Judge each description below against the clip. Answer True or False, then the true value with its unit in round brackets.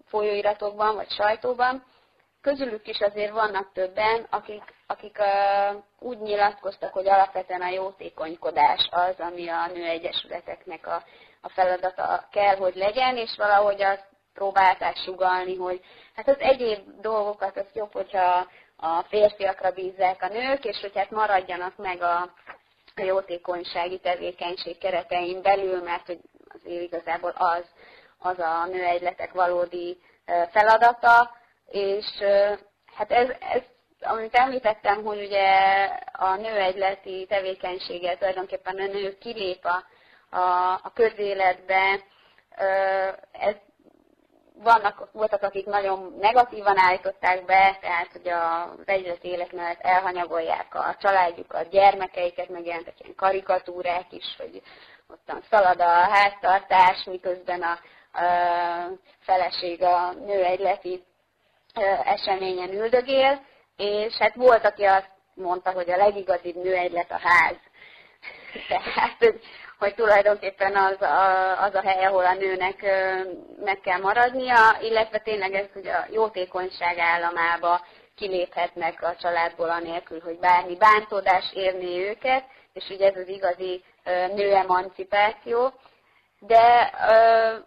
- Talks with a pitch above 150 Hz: True (190 Hz)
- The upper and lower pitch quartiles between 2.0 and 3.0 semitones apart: True (2.5 semitones)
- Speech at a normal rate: True (115 wpm)